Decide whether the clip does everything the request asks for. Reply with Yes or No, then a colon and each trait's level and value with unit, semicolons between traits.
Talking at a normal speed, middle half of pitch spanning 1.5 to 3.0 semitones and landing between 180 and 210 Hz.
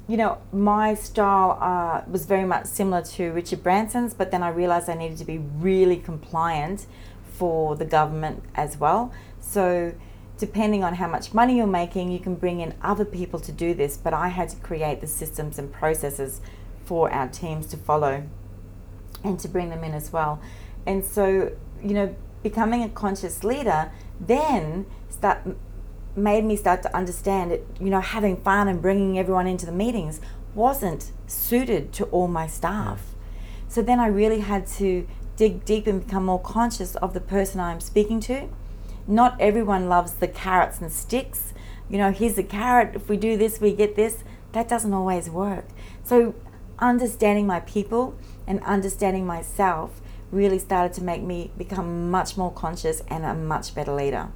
No: average, 175 wpm; average, 4.1 semitones; medium, 185 Hz